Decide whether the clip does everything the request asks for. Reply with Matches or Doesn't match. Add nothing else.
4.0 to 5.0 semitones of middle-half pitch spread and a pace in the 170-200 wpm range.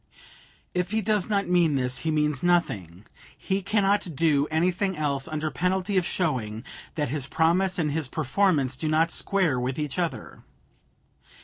Doesn't match